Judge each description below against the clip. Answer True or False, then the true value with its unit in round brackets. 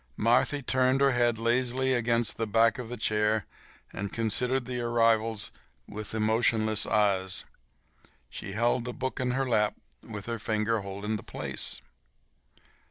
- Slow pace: False (145 wpm)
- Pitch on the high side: False (115 Hz)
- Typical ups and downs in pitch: False (2.3 semitones)